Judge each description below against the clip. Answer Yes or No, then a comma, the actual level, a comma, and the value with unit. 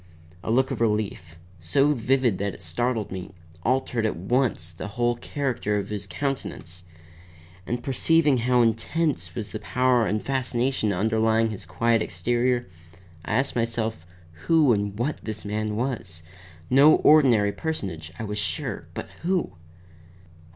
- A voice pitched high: No, low, 115 Hz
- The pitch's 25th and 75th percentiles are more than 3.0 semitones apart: Yes, average, 4.1 semitones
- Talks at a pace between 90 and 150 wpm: Yes, average, 145 wpm